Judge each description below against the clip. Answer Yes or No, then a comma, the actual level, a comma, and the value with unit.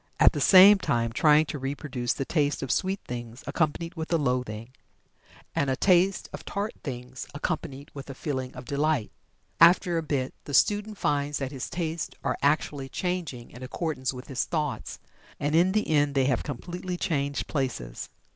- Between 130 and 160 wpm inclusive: No, average, 175 wpm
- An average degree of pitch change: Yes, average, 4.4 semitones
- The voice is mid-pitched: Yes, medium, 145 Hz